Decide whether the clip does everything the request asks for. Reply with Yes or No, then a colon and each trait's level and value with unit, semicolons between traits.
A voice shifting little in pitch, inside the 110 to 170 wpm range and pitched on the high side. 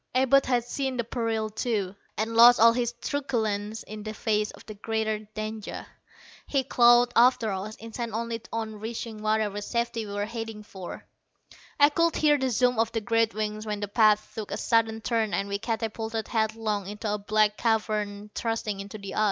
No: narrow, 1.8 semitones; average, 185 wpm; high, 220 Hz